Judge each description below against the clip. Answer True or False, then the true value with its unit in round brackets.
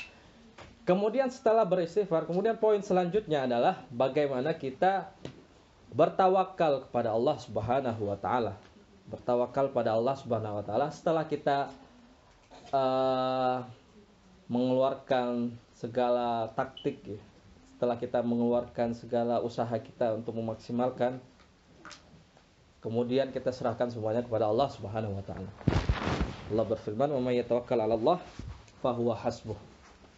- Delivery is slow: False (100 wpm)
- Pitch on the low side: True (125 Hz)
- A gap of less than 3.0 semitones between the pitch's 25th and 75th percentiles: False (3.5 semitones)